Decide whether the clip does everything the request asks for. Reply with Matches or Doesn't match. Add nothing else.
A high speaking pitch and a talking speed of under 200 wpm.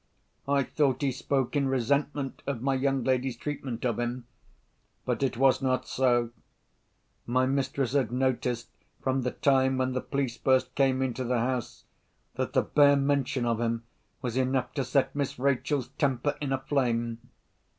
Doesn't match